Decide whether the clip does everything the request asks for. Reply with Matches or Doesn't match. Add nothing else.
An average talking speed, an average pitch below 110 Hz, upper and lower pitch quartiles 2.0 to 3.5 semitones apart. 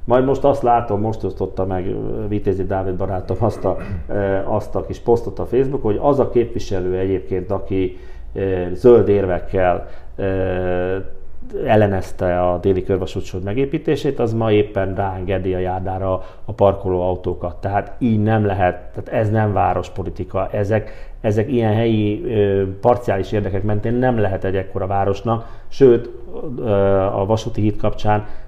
Matches